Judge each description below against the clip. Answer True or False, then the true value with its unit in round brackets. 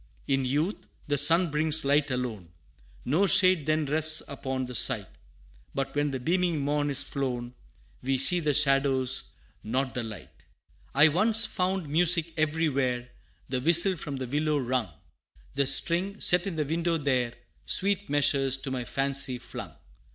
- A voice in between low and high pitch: True (145 Hz)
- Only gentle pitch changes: False (3.8 semitones)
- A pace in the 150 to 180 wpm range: True (160 wpm)